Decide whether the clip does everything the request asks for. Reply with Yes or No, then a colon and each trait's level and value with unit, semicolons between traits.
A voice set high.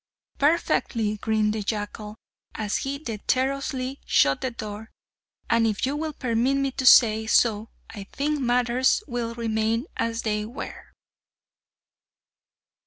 Yes: high, 230 Hz